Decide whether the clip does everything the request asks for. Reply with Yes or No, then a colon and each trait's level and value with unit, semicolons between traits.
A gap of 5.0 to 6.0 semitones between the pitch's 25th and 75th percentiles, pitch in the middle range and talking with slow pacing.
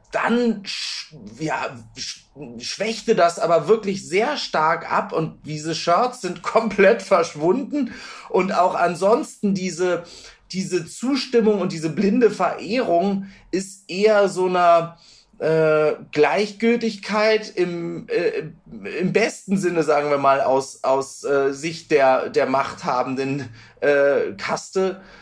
Yes: wide, 5.6 semitones; medium, 180 Hz; slow, 120 wpm